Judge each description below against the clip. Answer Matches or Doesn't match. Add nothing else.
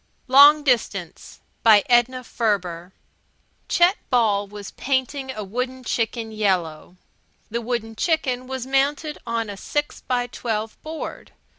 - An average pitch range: Matches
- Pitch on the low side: Doesn't match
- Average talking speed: Doesn't match